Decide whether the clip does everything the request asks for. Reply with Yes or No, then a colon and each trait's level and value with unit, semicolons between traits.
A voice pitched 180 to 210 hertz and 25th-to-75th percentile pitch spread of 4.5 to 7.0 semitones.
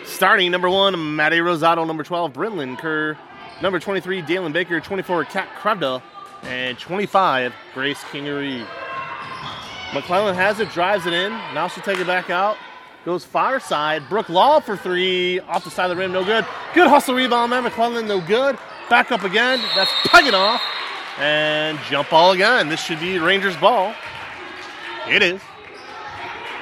Yes: medium, 185 Hz; average, 5.1 semitones